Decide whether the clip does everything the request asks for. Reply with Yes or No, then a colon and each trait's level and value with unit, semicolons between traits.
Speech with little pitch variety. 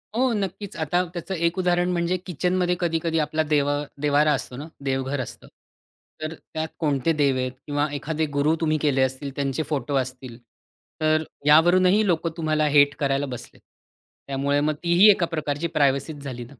No: average, 3.3 semitones